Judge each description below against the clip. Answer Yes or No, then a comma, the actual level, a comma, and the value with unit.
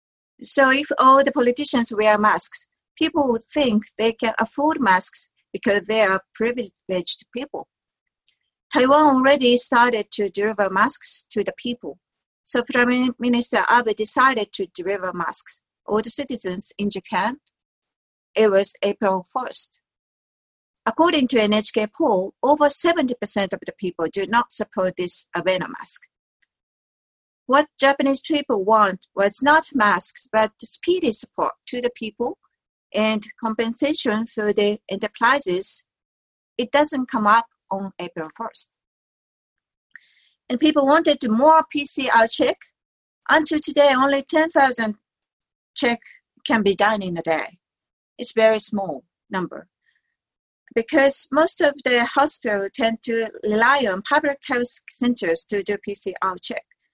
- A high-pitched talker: Yes, high, 230 Hz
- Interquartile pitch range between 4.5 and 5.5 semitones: Yes, average, 5.2 semitones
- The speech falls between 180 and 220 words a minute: No, slow, 135 wpm